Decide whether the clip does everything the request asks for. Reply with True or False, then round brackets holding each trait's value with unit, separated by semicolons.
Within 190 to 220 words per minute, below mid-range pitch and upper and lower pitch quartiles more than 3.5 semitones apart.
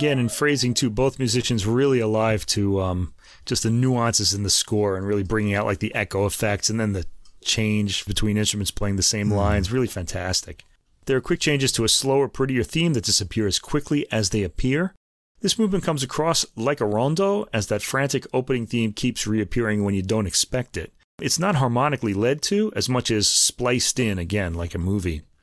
True (200 wpm; 110 Hz; 4.4 semitones)